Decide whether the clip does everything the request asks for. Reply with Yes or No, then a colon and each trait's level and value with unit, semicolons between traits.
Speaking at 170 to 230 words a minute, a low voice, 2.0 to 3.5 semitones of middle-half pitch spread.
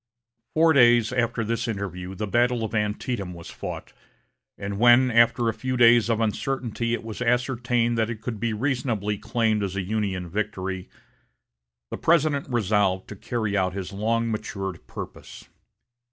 No: average, 155 wpm; low, 115 Hz; average, 3.1 semitones